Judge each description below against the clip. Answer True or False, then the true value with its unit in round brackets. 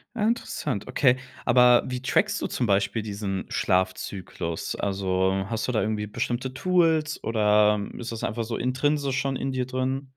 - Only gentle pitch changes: False (4.1 semitones)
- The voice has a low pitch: True (120 Hz)